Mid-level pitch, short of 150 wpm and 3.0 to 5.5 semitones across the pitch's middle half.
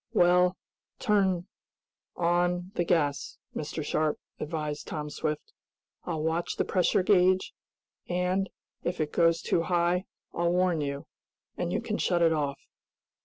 No: medium, 175 Hz; slow, 135 wpm; narrow, 2.6 semitones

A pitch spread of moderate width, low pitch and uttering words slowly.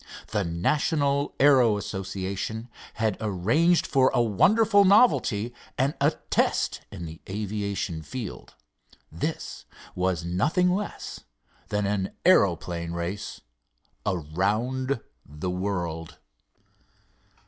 No: wide, 6.5 semitones; low, 105 Hz; slow, 95 wpm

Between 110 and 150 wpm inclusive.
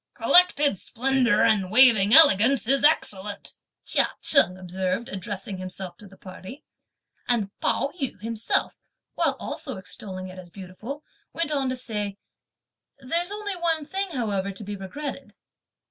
Yes: average, 140 wpm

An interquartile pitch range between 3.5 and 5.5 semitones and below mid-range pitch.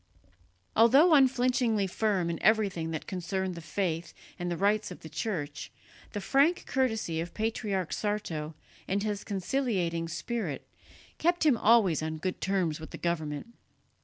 No: average, 5.0 semitones; high, 195 Hz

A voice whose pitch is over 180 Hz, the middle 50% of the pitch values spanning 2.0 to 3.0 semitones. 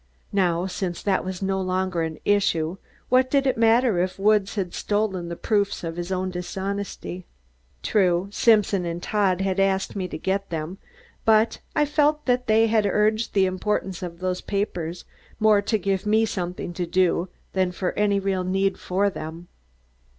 Yes: high, 190 Hz; average, 2.7 semitones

